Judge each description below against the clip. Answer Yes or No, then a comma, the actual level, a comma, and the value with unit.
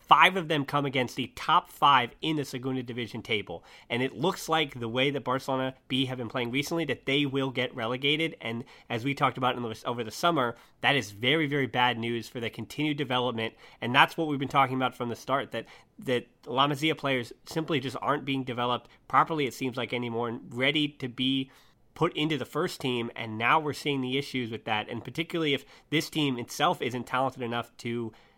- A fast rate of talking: Yes, fast, 220 wpm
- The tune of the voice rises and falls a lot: No, average, 3.1 semitones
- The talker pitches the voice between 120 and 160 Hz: Yes, low, 130 Hz